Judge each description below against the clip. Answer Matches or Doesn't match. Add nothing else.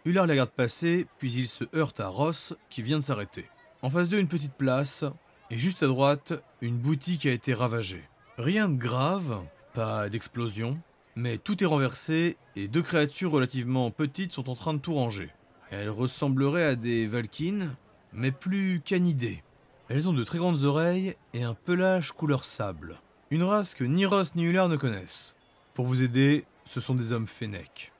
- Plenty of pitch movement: Matches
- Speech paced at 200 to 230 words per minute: Doesn't match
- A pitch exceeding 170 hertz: Doesn't match